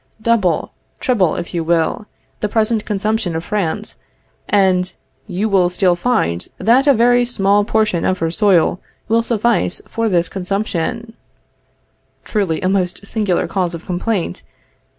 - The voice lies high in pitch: Yes, high, 200 Hz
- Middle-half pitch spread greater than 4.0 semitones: No, average, 3.7 semitones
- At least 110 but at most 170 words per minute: Yes, average, 140 wpm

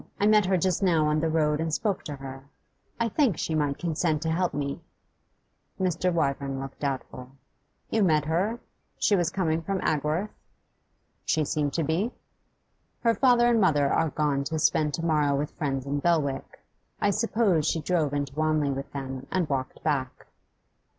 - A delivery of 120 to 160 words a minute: No, average, 175 wpm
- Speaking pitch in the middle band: Yes, medium, 155 Hz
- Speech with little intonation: No, average, 4.2 semitones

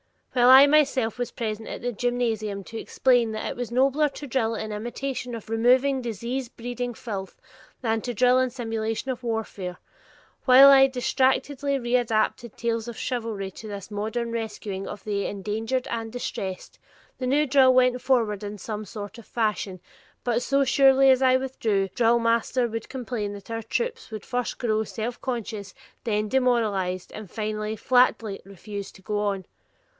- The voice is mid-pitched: No, high, 230 Hz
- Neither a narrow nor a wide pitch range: Yes, average, 3.1 semitones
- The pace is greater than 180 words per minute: No, average, 165 wpm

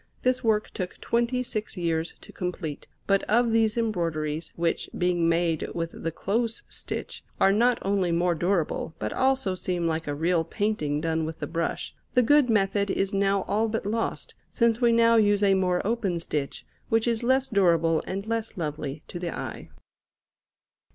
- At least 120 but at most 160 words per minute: No, average, 175 wpm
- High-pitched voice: Yes, high, 195 Hz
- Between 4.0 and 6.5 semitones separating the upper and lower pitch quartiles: Yes, average, 5.2 semitones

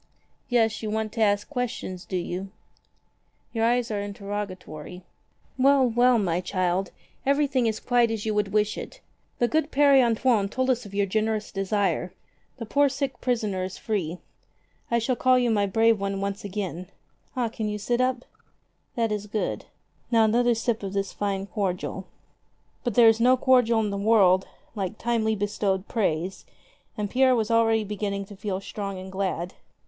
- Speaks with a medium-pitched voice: No, high, 215 Hz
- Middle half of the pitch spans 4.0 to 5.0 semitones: No, average, 3.3 semitones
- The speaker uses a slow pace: No, average, 175 wpm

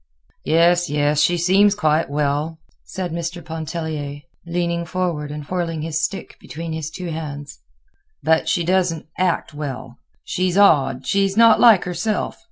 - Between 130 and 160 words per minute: Yes, average, 145 wpm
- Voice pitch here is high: No, medium, 165 Hz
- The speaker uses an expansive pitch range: No, average, 3.0 semitones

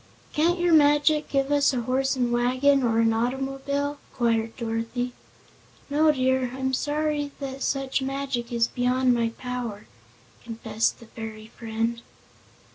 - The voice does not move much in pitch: No, average, 3.2 semitones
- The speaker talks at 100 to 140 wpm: Yes, slow, 135 wpm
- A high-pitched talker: Yes, very high, 255 Hz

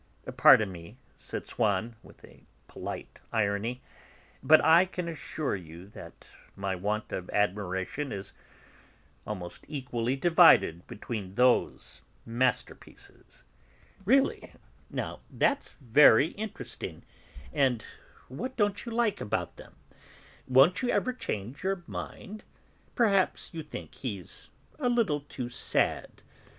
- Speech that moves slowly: Yes, slow, 115 wpm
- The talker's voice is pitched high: No, low, 130 Hz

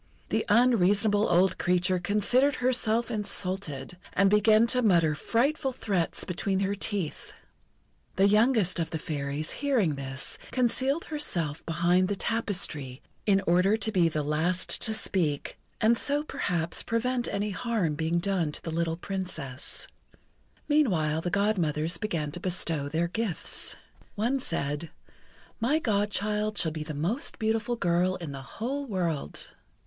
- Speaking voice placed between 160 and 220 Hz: Yes, high, 190 Hz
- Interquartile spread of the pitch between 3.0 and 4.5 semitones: No, average, 5.2 semitones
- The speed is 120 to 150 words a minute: Yes, average, 140 wpm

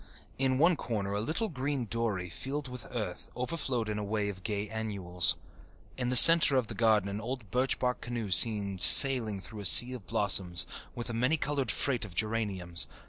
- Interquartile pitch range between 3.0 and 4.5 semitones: Yes, average, 4.1 semitones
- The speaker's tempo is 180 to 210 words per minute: Yes, average, 195 wpm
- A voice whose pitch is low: Yes, low, 115 Hz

